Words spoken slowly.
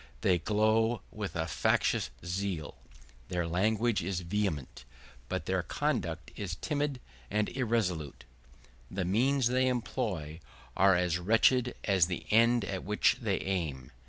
Yes: slow, 130 wpm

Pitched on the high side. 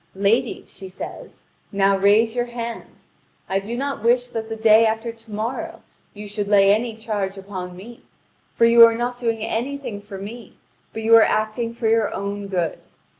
Yes: high, 220 Hz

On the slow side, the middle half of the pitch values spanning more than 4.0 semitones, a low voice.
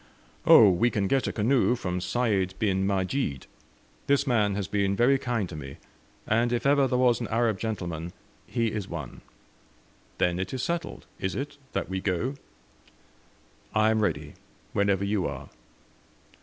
No: average, 160 wpm; average, 4.6 semitones; low, 105 Hz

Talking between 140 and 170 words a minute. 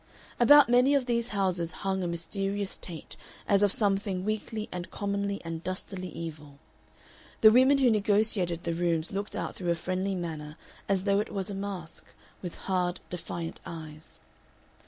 Yes: average, 160 wpm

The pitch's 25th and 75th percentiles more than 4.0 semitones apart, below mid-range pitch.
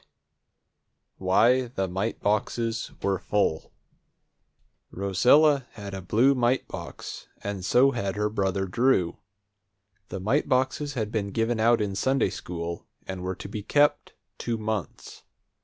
Yes: average, 4.4 semitones; low, 105 Hz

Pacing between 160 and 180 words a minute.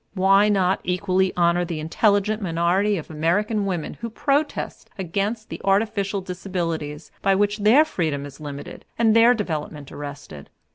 No: average, 145 wpm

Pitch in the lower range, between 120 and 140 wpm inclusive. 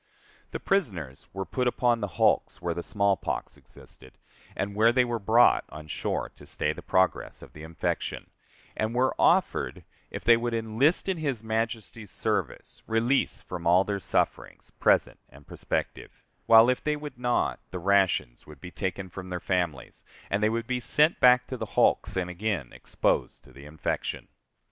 No: low, 110 Hz; average, 175 wpm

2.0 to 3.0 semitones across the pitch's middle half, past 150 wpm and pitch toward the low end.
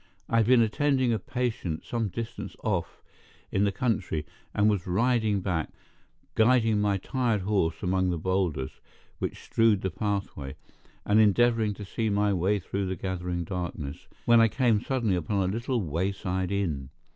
No: average, 3.8 semitones; average, 160 wpm; low, 100 Hz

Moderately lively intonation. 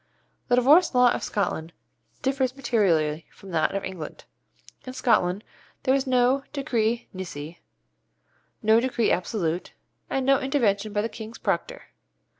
No: wide, 5.7 semitones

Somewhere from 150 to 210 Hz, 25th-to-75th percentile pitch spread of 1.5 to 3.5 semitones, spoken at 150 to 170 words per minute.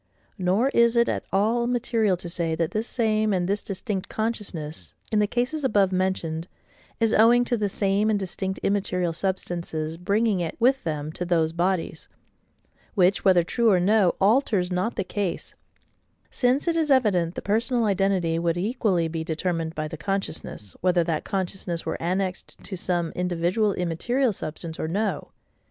No: high, 190 Hz; average, 4.1 semitones; average, 165 wpm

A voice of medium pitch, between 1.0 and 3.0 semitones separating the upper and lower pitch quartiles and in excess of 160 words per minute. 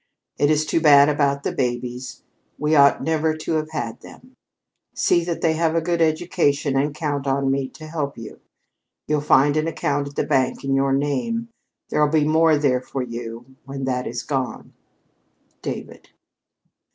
Yes: medium, 145 Hz; average, 2.7 semitones; average, 175 wpm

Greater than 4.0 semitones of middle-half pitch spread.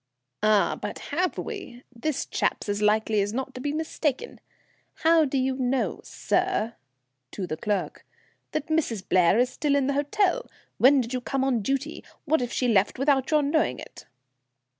Yes: average, 5.3 semitones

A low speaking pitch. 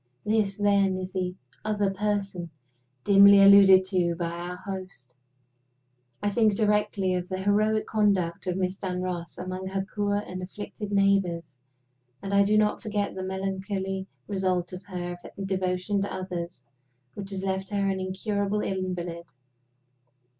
No: high, 190 Hz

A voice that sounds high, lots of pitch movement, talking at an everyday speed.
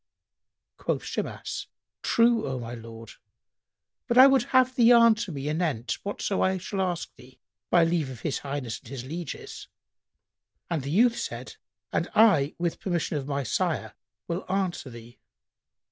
No: medium, 165 Hz; wide, 7.4 semitones; average, 155 wpm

